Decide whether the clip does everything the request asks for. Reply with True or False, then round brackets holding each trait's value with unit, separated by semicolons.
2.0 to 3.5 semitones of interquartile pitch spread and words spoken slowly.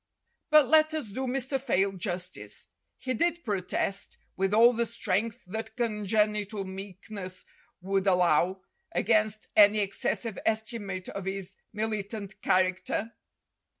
True (3.0 semitones; 120 wpm)